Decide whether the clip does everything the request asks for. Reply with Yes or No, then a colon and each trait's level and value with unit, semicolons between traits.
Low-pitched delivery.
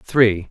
Yes: low, 110 Hz